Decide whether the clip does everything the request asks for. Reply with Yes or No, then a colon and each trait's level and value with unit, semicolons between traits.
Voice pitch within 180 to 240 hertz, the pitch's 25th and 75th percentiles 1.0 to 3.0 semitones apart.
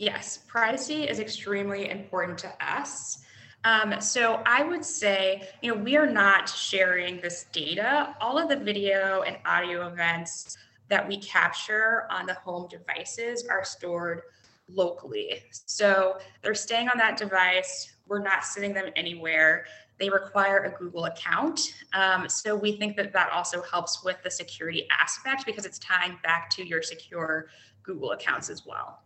No: high, 190 Hz; average, 3.7 semitones